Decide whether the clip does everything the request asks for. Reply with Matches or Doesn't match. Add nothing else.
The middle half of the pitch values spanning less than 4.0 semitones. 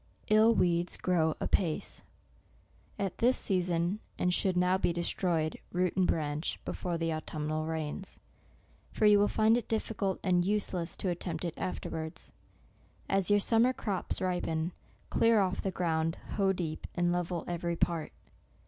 Matches